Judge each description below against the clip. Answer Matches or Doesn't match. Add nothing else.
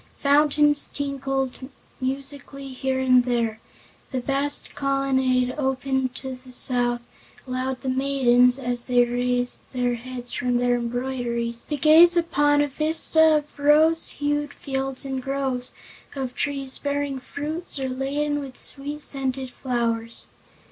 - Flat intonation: Matches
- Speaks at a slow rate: Matches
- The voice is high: Matches